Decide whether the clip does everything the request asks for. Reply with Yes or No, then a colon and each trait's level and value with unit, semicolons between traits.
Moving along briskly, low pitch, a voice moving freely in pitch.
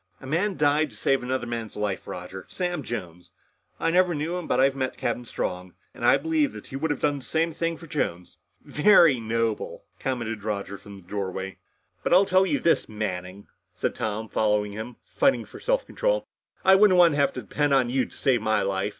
Yes: fast, 210 wpm; low, 130 Hz; wide, 7.9 semitones